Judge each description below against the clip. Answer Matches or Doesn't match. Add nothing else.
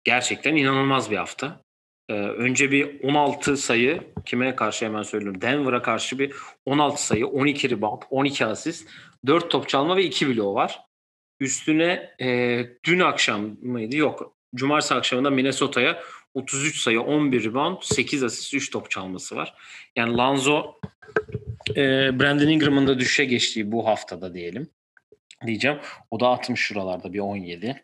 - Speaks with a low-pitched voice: Matches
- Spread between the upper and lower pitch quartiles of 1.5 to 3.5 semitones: Doesn't match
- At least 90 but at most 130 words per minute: Doesn't match